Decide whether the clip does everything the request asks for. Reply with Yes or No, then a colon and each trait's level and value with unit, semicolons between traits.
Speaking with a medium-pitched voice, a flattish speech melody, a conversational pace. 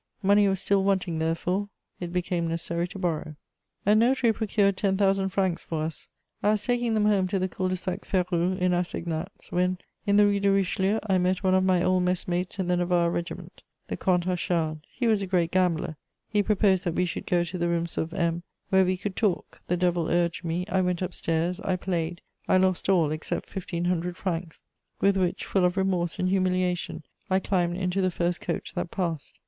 No: medium, 180 Hz; narrow, 1.9 semitones; fast, 210 wpm